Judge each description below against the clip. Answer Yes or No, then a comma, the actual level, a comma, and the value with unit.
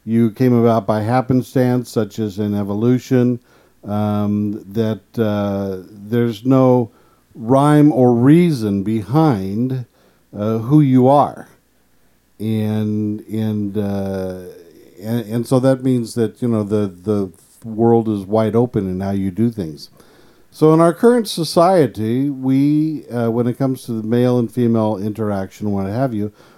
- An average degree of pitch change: Yes, average, 3.3 semitones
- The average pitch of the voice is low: Yes, low, 115 Hz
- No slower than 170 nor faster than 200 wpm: No, average, 140 wpm